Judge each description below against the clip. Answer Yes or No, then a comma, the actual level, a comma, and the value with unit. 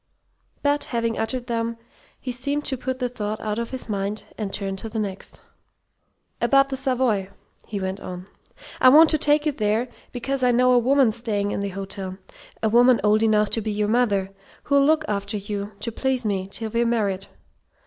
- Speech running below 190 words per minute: No, average, 195 wpm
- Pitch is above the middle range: Yes, high, 230 Hz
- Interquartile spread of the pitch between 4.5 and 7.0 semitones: No, average, 3.9 semitones